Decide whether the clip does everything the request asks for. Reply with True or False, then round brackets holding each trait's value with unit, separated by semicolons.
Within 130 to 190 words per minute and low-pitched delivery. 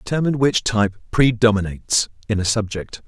True (135 wpm; 110 Hz)